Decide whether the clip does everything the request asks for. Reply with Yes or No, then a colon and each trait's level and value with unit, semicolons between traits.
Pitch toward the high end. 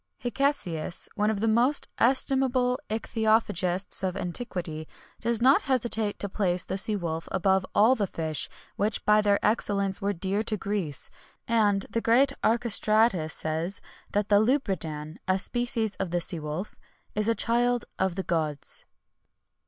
Yes: high, 205 Hz